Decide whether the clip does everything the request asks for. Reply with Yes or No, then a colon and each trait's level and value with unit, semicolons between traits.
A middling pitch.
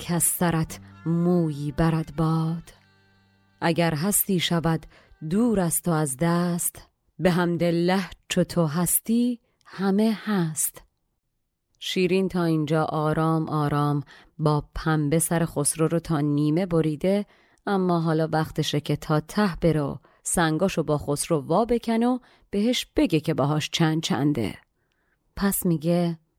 Yes: medium, 165 Hz